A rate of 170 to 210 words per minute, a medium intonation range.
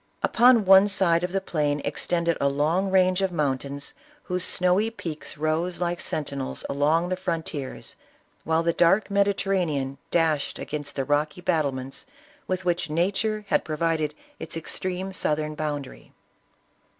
No: average, 140 wpm; average, 3.7 semitones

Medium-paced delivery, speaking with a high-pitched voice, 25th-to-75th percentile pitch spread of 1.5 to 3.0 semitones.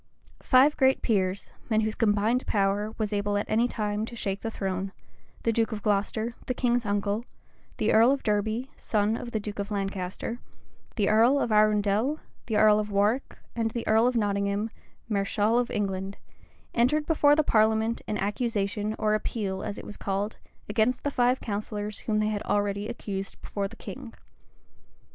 Yes: average, 175 wpm; high, 215 Hz; narrow, 2.4 semitones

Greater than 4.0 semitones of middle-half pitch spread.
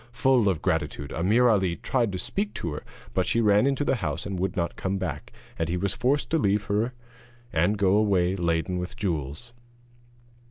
Yes: average, 4.9 semitones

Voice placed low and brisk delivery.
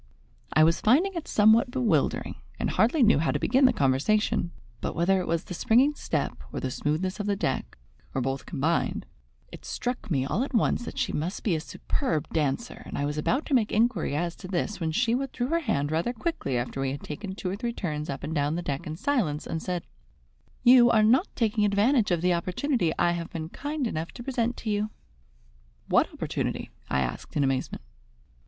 No: high, 190 Hz; fast, 210 wpm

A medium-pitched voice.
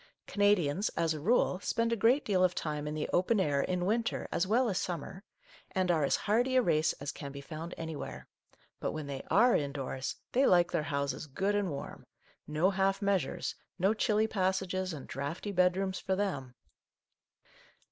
Yes: medium, 180 Hz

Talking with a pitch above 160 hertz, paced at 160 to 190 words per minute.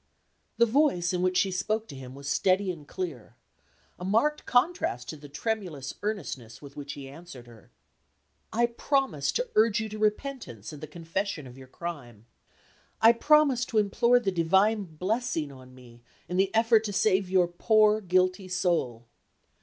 Yes: medium, 185 Hz; average, 170 wpm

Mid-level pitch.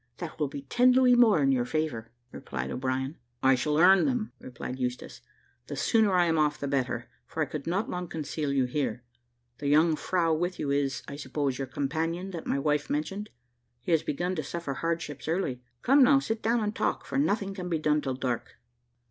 Yes: medium, 155 Hz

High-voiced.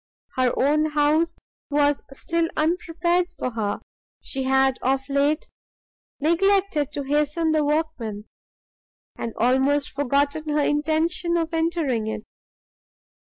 Yes: very high, 295 Hz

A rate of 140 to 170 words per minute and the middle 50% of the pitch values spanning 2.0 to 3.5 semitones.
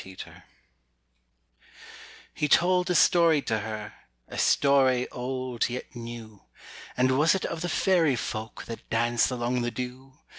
No: average, 150 wpm; average, 3.9 semitones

